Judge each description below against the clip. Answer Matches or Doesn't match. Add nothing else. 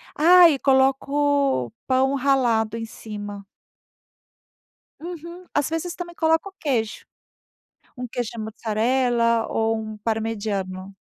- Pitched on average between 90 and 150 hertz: Doesn't match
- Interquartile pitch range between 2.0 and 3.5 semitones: Doesn't match